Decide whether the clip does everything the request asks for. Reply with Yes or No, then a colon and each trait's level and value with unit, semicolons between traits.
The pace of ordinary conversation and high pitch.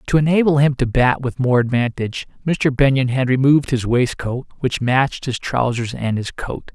No: average, 185 wpm; low, 130 Hz